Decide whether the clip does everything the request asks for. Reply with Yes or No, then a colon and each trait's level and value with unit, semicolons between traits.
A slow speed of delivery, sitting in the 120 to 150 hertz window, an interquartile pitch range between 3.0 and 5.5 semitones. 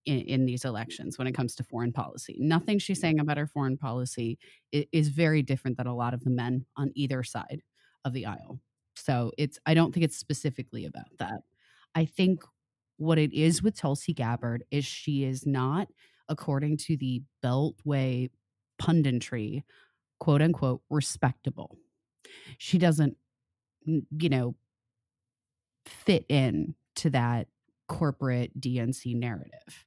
No: average, 145 wpm; low, 135 Hz; average, 3.8 semitones